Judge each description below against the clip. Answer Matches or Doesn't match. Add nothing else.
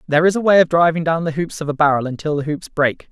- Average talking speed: Doesn't match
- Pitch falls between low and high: Matches